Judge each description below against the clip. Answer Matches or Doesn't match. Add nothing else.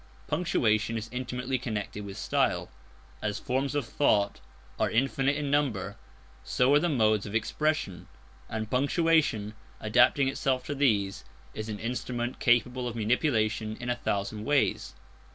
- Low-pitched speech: Matches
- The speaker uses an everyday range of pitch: Matches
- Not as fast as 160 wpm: Matches